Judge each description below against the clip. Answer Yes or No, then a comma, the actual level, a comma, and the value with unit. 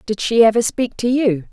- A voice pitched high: Yes, high, 225 Hz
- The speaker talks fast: Yes, fast, 235 wpm